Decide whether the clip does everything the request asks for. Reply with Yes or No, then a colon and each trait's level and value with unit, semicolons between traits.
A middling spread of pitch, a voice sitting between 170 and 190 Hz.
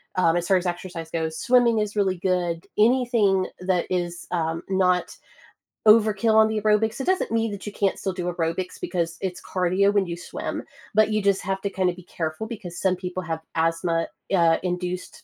Yes: average, 3.3 semitones; medium, 185 Hz